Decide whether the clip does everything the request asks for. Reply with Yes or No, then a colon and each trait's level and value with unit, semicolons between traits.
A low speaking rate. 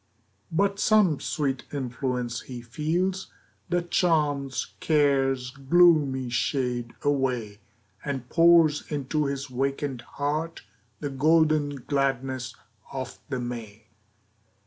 Yes: slow, 100 wpm